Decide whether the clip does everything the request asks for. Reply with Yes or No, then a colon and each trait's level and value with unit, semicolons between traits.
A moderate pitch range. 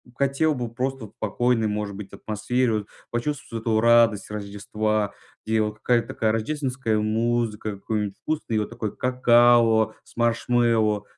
No: narrow, 2.2 semitones